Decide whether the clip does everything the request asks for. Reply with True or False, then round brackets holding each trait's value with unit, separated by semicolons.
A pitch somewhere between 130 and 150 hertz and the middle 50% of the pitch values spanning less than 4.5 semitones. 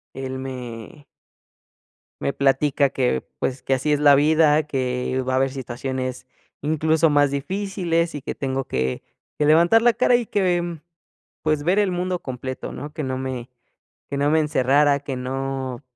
True (140 Hz; 3.3 semitones)